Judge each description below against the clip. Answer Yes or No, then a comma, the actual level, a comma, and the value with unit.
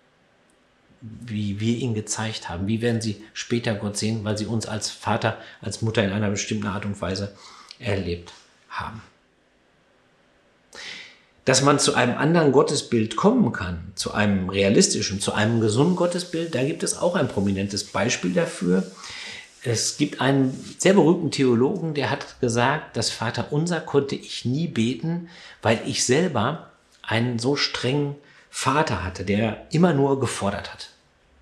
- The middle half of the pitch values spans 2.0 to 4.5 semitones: No, average, 5.0 semitones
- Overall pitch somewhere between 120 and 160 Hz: No, low, 110 Hz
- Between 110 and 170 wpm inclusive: Yes, average, 150 wpm